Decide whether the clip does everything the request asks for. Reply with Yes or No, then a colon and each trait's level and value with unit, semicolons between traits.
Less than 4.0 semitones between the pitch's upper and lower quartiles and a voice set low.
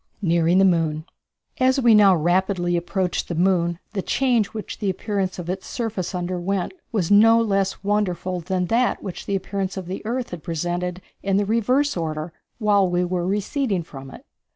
No: average, 2.9 semitones; high, 190 Hz